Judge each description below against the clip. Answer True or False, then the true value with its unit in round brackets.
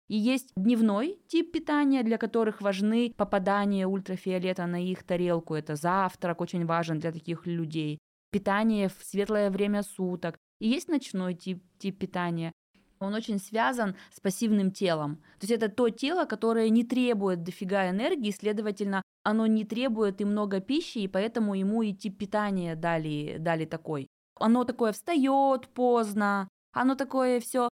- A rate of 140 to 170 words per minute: True (150 wpm)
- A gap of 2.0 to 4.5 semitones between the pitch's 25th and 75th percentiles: True (3.9 semitones)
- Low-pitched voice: False (205 Hz)